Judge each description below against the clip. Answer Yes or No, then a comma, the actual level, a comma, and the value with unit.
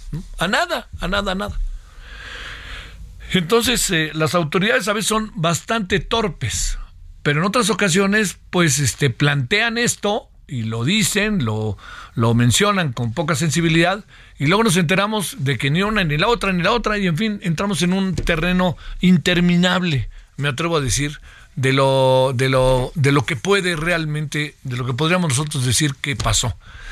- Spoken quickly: No, average, 165 wpm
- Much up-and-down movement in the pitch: Yes, wide, 6.6 semitones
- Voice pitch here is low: No, medium, 165 Hz